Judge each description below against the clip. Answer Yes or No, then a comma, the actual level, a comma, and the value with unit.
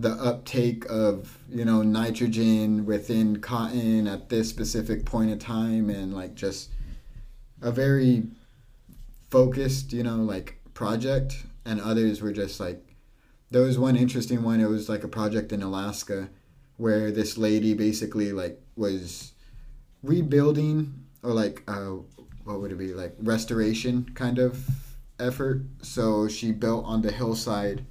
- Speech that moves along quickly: No, average, 140 wpm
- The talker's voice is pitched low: Yes, low, 115 Hz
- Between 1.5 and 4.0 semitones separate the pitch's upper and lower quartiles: Yes, average, 2.8 semitones